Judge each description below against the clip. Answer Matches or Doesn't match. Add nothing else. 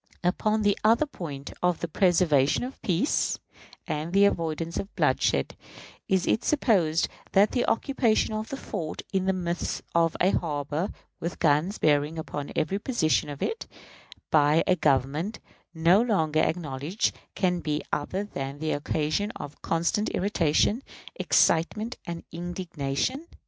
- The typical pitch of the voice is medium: Matches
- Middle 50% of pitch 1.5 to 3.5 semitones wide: Doesn't match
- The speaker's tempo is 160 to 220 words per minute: Doesn't match